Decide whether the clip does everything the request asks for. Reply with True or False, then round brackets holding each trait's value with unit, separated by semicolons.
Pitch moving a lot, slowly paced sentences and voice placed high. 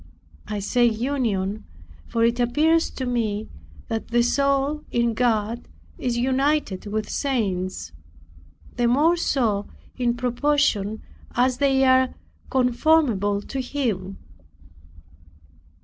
False (4.0 semitones; 105 wpm; 240 Hz)